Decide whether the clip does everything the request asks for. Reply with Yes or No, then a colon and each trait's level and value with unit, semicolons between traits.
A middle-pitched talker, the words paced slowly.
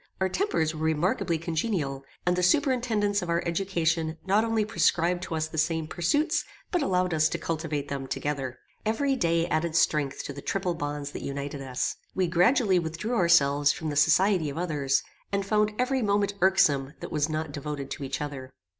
No: medium, 165 Hz; average, 185 wpm